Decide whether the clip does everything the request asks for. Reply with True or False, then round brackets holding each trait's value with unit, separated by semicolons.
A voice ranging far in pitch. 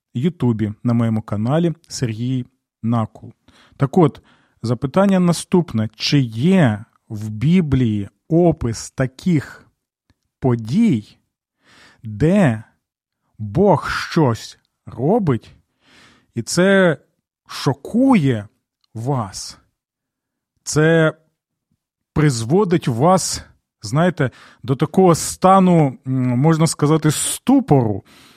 True (6.0 semitones)